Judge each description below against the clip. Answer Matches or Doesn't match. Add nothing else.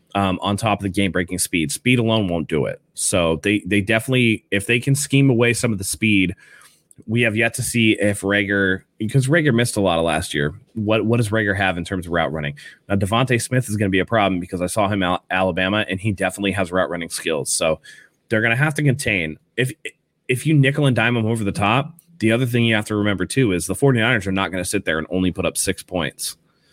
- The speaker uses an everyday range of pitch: Matches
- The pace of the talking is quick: Matches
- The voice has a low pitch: Matches